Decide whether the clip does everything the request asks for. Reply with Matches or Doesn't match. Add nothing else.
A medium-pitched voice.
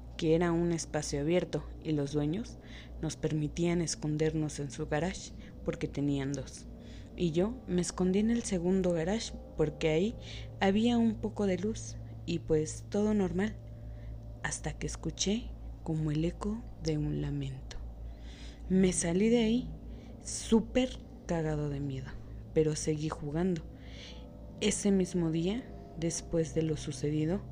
Matches